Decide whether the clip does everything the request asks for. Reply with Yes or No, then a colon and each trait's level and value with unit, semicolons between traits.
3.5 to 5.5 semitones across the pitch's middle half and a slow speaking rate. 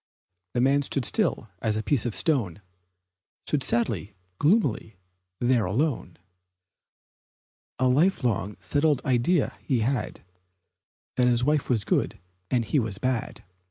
Yes: average, 4.2 semitones; slow, 130 wpm